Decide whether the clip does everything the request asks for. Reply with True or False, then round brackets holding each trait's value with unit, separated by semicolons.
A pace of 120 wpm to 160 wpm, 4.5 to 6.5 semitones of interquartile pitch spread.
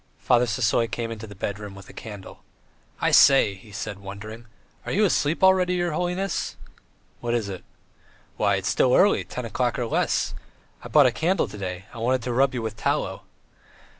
False (190 wpm; 5.1 semitones)